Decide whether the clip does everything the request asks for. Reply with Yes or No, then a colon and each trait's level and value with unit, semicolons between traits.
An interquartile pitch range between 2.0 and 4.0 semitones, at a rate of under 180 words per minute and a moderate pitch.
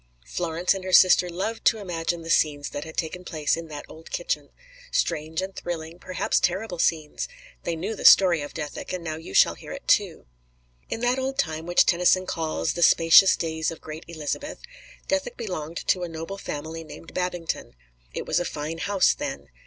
No: average, 2.8 semitones; average, 190 wpm; medium, 170 Hz